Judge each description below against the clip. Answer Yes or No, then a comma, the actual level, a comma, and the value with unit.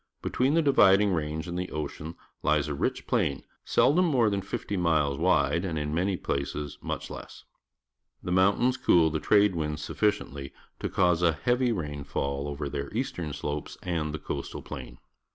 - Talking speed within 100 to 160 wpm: No, average, 185 wpm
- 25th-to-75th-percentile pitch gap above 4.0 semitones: Yes, average, 5.2 semitones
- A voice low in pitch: Yes, very low, 85 Hz